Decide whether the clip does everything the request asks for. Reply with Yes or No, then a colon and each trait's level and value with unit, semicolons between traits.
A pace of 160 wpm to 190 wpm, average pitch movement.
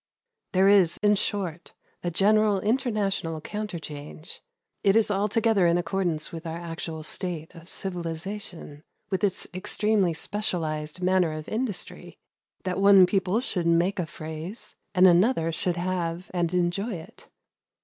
No: slow, 135 wpm; average, 3.4 semitones